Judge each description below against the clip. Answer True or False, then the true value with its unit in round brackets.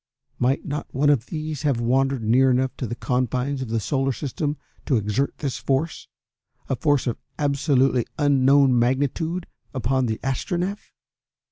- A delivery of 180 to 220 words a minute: False (150 wpm)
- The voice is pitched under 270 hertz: True (135 Hz)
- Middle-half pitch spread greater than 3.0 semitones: False (2.5 semitones)